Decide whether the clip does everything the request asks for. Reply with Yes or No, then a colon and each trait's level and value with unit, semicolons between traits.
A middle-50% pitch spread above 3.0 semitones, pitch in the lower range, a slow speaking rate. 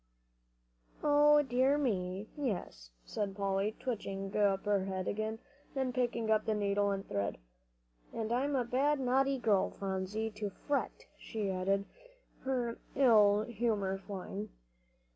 No: average, 4.3 semitones; high, 215 Hz; slow, 130 wpm